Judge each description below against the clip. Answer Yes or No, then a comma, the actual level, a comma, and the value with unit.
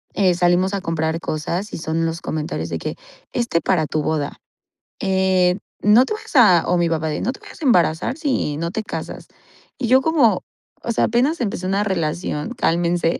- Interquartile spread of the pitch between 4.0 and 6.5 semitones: Yes, average, 5.1 semitones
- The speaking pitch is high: No, medium, 180 Hz